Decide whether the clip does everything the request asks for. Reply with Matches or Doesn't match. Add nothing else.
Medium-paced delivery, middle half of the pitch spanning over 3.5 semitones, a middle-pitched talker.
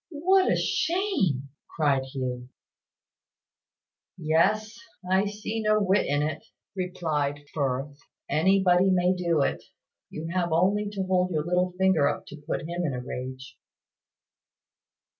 Doesn't match